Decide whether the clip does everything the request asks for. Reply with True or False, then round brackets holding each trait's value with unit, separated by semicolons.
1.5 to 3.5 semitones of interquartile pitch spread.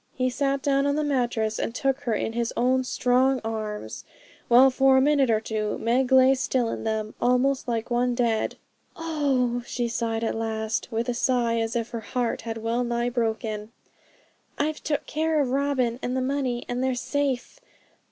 True (2.6 semitones)